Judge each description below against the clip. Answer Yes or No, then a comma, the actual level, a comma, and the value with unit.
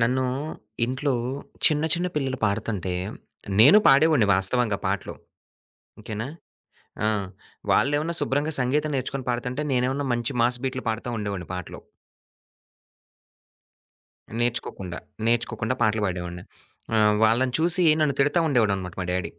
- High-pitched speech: No, low, 120 Hz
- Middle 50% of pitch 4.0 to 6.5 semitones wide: Yes, average, 4.6 semitones